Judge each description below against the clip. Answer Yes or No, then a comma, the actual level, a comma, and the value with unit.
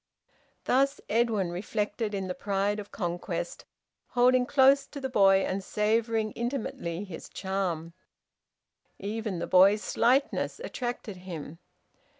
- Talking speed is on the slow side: Yes, slow, 120 wpm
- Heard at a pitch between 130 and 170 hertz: No, high, 210 Hz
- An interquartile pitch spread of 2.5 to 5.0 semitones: Yes, average, 4.3 semitones